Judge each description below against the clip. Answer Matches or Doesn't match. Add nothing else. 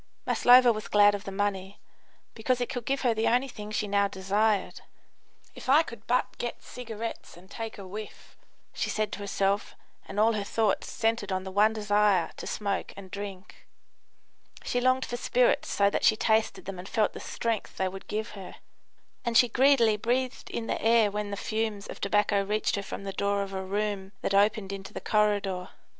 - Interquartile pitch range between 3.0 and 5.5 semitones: Doesn't match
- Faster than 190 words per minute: Matches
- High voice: Matches